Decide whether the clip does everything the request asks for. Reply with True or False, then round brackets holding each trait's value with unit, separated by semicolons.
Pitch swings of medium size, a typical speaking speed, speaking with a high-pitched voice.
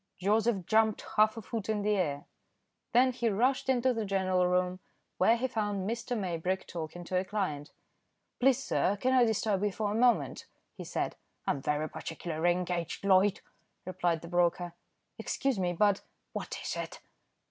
True (4.0 semitones; 170 wpm; 195 Hz)